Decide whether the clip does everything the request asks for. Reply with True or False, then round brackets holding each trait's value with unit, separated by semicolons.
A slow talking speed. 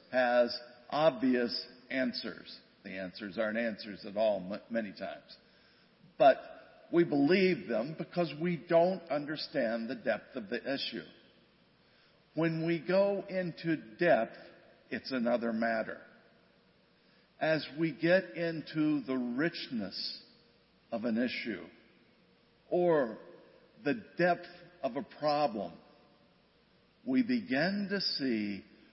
True (110 wpm)